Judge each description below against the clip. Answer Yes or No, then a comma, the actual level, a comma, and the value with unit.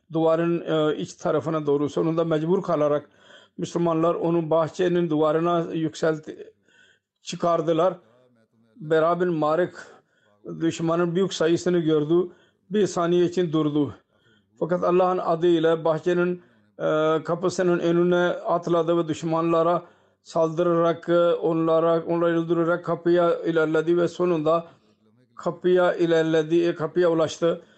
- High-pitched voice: No, medium, 170 Hz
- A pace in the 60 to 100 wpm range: Yes, slow, 95 wpm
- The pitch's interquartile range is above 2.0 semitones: No, narrow, 1.5 semitones